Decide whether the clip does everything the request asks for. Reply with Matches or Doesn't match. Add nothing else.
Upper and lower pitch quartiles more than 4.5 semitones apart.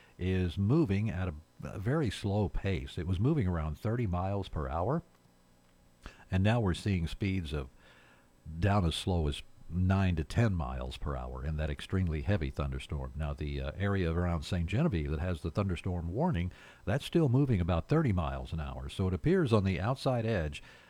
Matches